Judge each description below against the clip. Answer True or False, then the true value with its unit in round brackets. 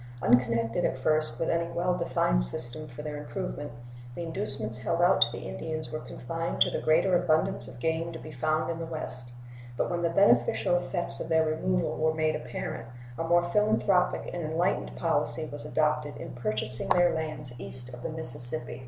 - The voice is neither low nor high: True (155 Hz)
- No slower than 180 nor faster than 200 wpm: True (190 wpm)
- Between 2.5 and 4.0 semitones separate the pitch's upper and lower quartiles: False (5.5 semitones)